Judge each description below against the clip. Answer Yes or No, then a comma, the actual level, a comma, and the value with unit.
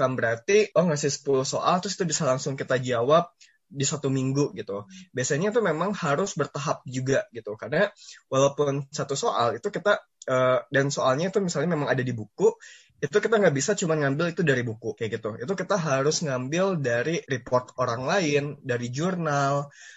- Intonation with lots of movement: Yes, wide, 6.0 semitones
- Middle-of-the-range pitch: Yes, medium, 145 Hz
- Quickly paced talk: Yes, fast, 175 wpm